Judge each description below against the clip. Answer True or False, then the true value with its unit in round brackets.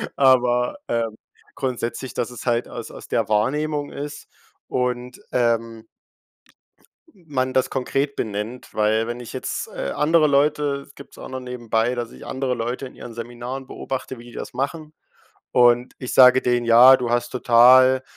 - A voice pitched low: True (125 Hz)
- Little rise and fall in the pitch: True (2.0 semitones)